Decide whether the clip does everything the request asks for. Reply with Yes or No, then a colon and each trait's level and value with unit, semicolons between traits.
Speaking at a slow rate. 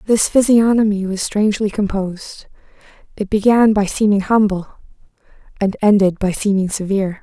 Yes: slow, 125 wpm